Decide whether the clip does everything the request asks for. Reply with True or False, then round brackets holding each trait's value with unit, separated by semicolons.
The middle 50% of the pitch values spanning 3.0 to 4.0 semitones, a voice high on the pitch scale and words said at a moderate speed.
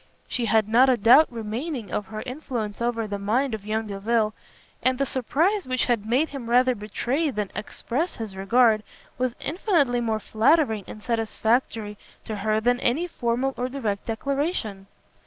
True (3.4 semitones; 235 Hz; 165 wpm)